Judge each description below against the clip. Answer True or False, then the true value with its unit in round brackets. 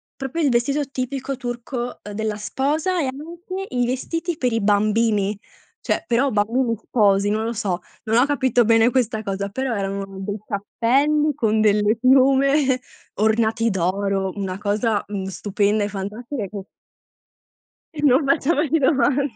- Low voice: False (230 Hz)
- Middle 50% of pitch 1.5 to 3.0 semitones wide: False (4.6 semitones)